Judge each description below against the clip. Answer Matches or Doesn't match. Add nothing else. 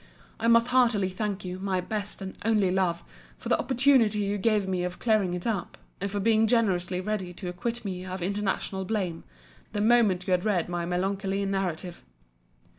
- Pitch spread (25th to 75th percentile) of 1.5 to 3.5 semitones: Matches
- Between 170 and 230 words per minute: Matches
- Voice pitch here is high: Matches